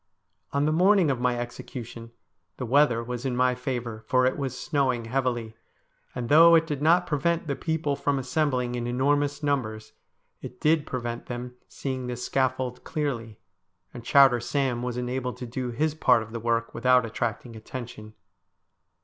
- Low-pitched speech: Yes, low, 125 Hz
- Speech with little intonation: No, average, 3.1 semitones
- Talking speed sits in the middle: Yes, average, 165 wpm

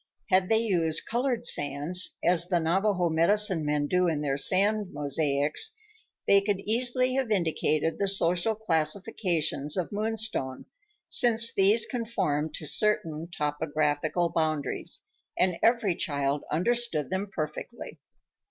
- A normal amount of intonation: No, wide, 5.7 semitones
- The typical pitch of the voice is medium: Yes, medium, 180 Hz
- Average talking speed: No, slow, 125 wpm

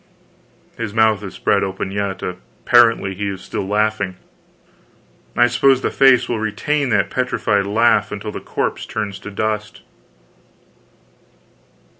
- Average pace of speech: No, slow, 130 wpm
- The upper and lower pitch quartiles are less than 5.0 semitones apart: Yes, average, 2.7 semitones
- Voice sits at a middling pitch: No, low, 105 Hz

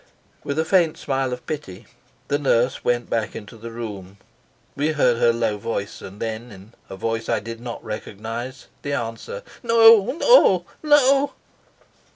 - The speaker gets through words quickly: No, average, 160 wpm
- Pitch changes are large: Yes, wide, 5.9 semitones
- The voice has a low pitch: Yes, low, 120 Hz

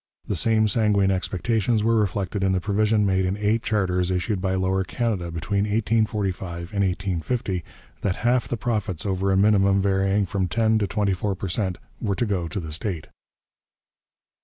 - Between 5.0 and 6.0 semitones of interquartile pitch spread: No, narrow, 2.4 semitones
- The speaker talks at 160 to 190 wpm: Yes, average, 175 wpm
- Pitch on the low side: Yes, low, 100 Hz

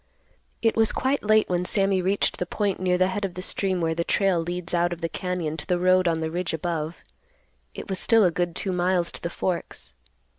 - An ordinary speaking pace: No, fast, 230 wpm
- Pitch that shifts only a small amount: Yes, narrow, 2.0 semitones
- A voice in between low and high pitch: Yes, medium, 180 Hz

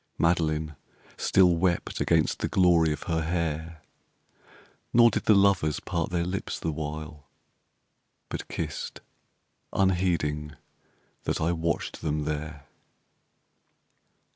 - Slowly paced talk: Yes, slow, 110 wpm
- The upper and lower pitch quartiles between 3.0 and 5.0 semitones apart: No, narrow, 2.4 semitones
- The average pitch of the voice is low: Yes, very low, 80 Hz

